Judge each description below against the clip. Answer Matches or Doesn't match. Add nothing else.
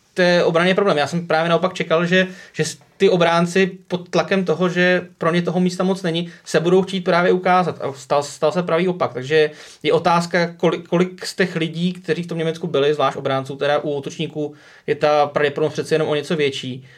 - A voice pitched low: Doesn't match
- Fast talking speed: Matches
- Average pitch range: Matches